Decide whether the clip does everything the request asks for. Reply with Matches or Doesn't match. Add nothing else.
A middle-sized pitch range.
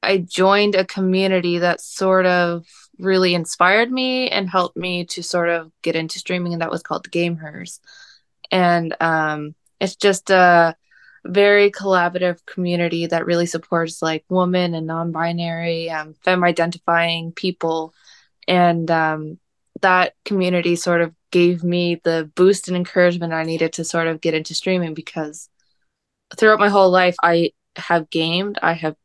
Doesn't match